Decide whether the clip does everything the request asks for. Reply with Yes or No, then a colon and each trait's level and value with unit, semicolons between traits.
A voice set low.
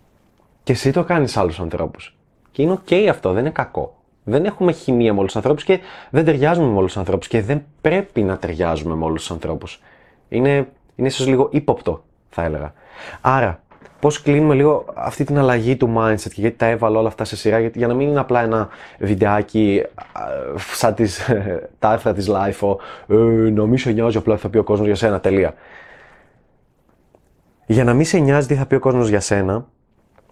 Yes: low, 115 Hz